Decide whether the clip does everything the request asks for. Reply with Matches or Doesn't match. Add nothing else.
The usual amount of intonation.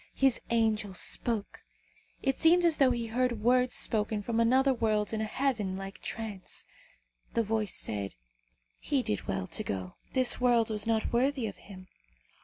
Matches